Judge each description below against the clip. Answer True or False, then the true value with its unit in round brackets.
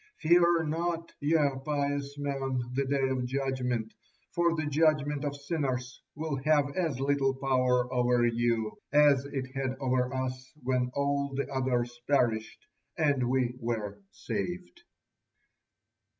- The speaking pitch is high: False (135 Hz)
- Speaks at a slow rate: True (130 wpm)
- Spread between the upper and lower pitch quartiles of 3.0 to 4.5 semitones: False (2.6 semitones)